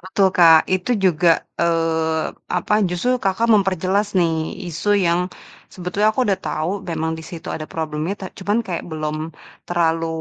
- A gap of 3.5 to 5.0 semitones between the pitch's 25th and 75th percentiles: No, average, 3.0 semitones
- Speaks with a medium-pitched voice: Yes, medium, 170 Hz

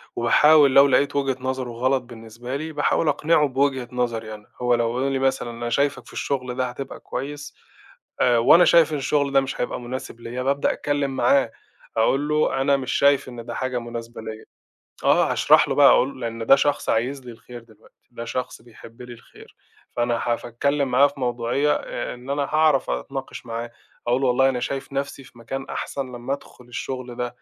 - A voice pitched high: No, low, 130 Hz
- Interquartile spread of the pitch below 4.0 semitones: Yes, narrow, 2.6 semitones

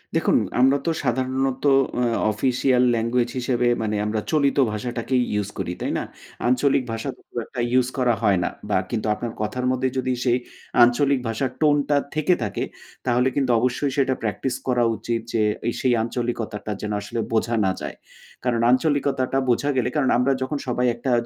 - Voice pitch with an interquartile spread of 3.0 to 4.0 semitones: No, narrow, 2.4 semitones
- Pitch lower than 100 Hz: No, low, 125 Hz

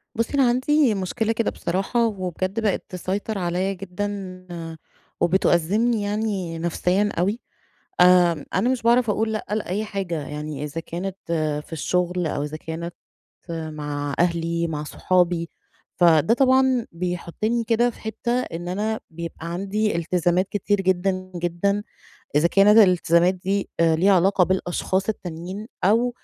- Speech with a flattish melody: No, average, 3.8 semitones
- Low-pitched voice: No, medium, 185 Hz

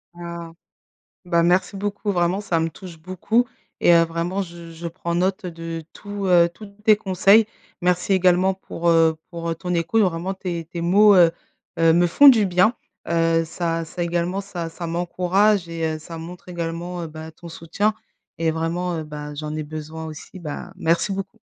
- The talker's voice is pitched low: No, medium, 170 Hz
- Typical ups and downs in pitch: No, narrow, 2.2 semitones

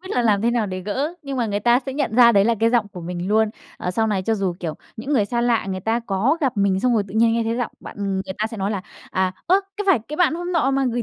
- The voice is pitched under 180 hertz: No, high, 225 Hz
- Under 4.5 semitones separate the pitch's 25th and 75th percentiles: Yes, average, 4.0 semitones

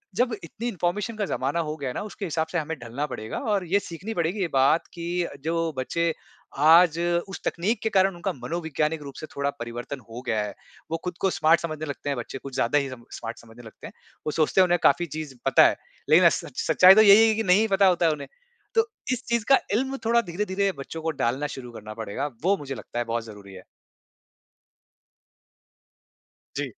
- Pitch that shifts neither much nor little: No, wide, 6.6 semitones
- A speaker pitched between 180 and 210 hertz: No, medium, 160 Hz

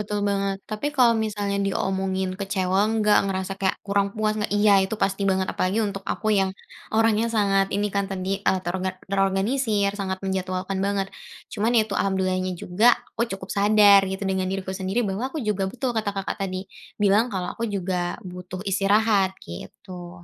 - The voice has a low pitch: No, high, 195 Hz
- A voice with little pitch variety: Yes, narrow, 1.8 semitones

